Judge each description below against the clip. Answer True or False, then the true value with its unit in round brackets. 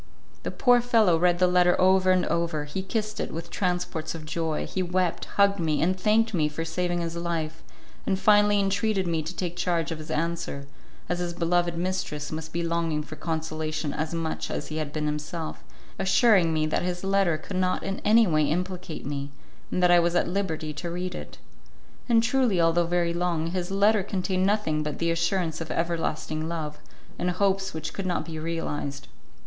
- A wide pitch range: False (2.8 semitones)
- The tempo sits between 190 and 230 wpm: True (195 wpm)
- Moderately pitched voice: True (170 Hz)